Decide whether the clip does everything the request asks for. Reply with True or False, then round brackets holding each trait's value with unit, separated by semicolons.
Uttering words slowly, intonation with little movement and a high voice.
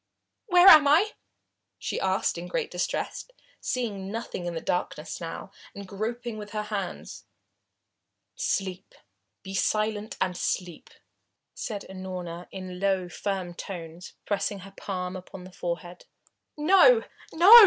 False (130 wpm; 3.3 semitones; 195 Hz)